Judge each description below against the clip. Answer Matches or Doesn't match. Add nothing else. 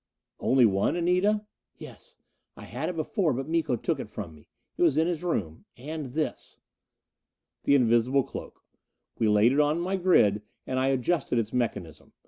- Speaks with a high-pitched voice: Doesn't match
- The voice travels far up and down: Matches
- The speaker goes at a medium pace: Matches